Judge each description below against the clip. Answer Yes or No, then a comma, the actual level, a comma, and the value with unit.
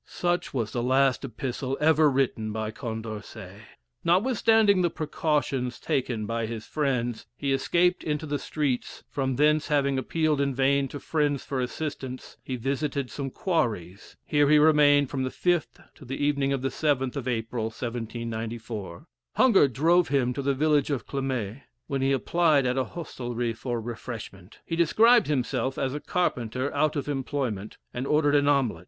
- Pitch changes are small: No, average, 3.7 semitones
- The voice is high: No, low, 135 Hz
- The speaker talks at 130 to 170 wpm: Yes, average, 165 wpm